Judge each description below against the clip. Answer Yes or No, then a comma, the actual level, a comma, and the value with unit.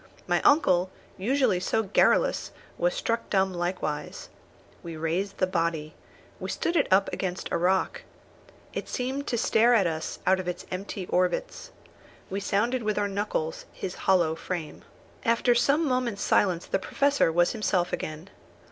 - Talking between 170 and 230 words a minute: No, average, 155 wpm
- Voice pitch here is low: No, high, 190 Hz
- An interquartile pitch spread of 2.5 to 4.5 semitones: No, average, 5.0 semitones